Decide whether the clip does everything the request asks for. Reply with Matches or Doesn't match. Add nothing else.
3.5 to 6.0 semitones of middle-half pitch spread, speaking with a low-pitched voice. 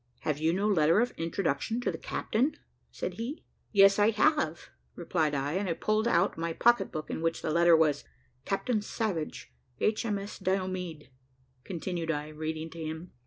Doesn't match